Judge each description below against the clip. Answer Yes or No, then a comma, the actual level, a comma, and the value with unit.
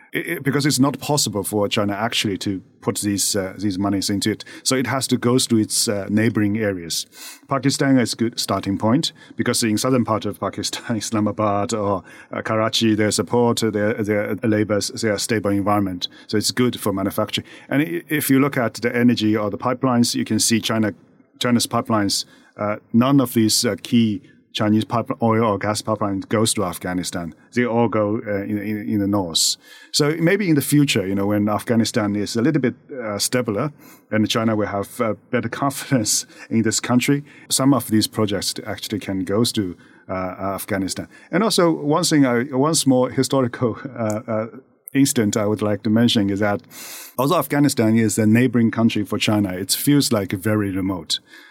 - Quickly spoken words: No, average, 185 wpm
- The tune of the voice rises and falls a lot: No, average, 3.2 semitones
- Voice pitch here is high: No, low, 110 Hz